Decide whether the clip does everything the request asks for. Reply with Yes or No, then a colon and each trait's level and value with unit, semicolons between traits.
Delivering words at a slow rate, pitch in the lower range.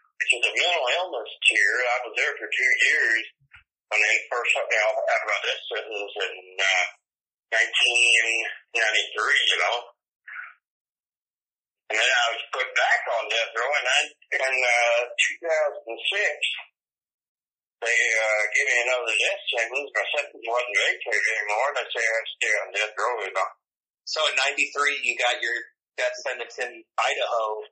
No: average, 155 wpm; low, 120 Hz